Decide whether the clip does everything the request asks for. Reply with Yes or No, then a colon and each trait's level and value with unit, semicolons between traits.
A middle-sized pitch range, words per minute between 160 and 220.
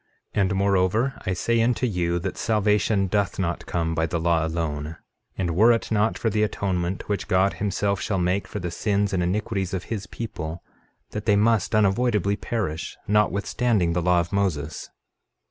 Yes: average, 3.3 semitones; average, 180 wpm